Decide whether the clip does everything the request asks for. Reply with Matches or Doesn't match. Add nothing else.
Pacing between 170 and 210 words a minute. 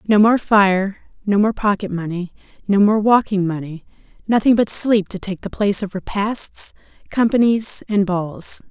Doesn't match